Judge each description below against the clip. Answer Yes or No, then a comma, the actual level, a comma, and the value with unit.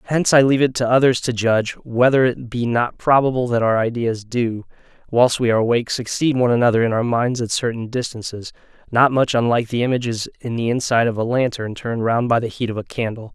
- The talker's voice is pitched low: Yes, low, 120 Hz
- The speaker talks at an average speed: No, fast, 220 wpm